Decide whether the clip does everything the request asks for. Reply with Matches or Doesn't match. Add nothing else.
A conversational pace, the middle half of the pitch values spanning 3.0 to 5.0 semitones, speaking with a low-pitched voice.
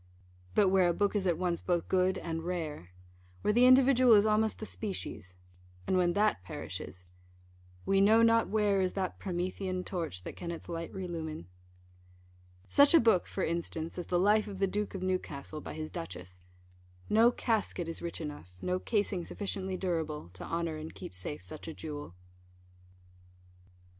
Doesn't match